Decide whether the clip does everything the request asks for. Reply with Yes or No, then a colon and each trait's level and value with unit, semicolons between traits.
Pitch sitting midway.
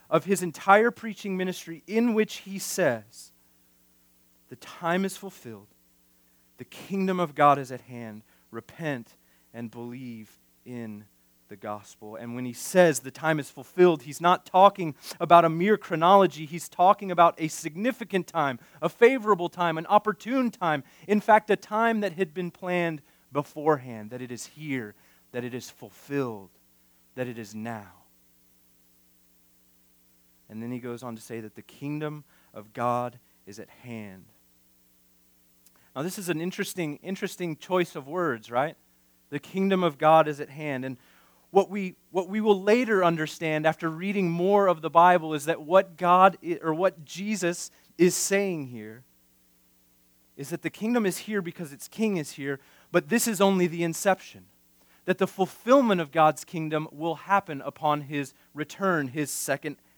Yes: medium, 155 Hz